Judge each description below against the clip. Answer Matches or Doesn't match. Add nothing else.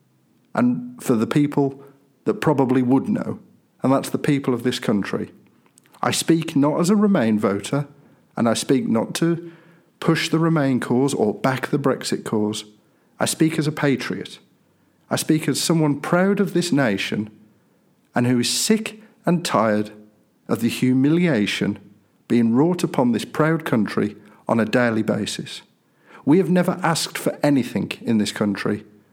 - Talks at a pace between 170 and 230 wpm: Doesn't match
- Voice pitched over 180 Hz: Doesn't match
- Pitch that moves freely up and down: Matches